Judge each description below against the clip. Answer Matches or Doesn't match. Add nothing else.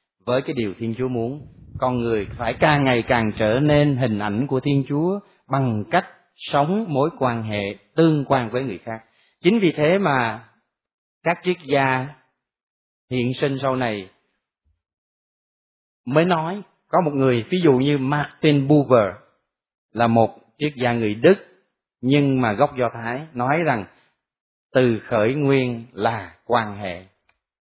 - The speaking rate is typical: Doesn't match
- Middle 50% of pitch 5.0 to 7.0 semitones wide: Doesn't match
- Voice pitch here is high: Doesn't match